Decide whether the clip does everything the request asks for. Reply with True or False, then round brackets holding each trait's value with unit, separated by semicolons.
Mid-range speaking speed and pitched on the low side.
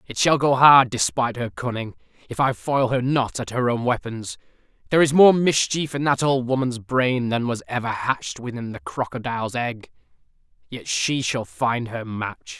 True (185 wpm; 120 Hz)